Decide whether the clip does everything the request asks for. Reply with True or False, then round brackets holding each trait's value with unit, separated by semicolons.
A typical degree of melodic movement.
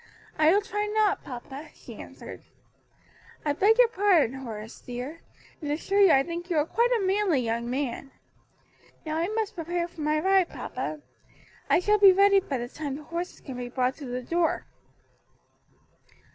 False (6.5 semitones)